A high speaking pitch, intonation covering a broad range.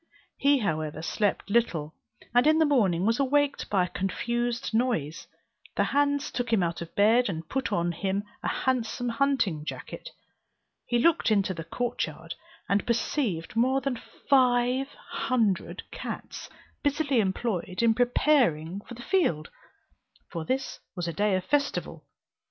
Yes: high, 230 Hz; wide, 6.1 semitones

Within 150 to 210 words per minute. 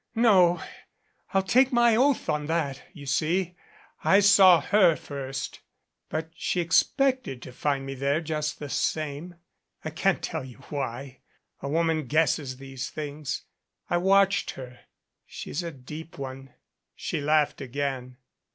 No: average, 140 wpm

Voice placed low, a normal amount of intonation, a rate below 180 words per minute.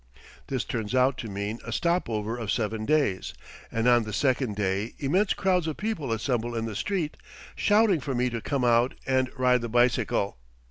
No: low, 120 Hz; average, 4.0 semitones; average, 190 wpm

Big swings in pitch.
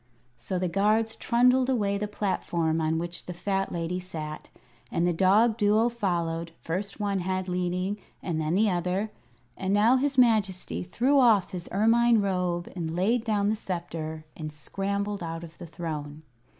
No: average, 3.8 semitones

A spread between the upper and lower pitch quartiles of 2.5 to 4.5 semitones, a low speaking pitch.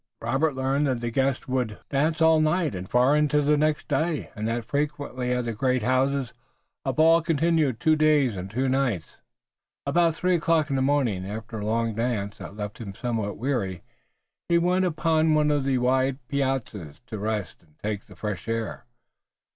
No: average, 5.1 semitones; low, 130 Hz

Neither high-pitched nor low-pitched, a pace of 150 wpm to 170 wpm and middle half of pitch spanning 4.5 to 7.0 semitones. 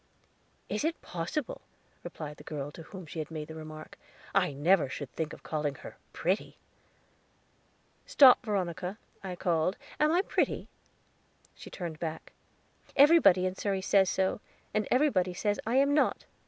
Yes: medium, 180 Hz; average, 155 wpm; average, 5.1 semitones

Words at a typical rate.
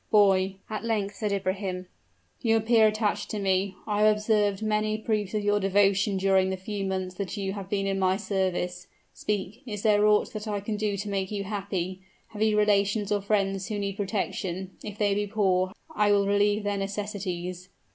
Yes: average, 195 wpm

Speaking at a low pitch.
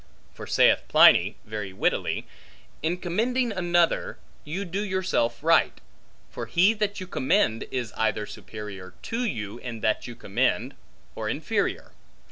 No: medium, 165 Hz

